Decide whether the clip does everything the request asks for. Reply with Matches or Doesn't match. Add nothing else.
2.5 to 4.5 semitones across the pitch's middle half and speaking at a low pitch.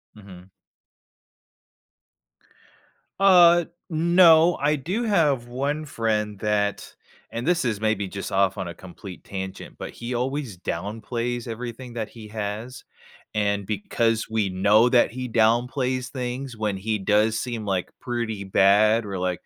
Matches